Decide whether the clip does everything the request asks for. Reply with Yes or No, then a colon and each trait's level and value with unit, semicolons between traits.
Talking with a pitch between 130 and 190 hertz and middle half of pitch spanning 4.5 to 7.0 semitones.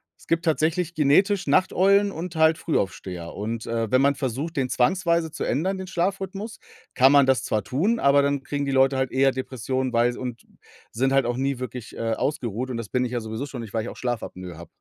Yes: low, 135 Hz; average, 5.2 semitones